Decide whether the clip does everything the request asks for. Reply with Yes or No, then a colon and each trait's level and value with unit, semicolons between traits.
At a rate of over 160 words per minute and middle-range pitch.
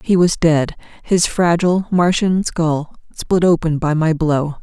No: average, 155 wpm; medium, 165 Hz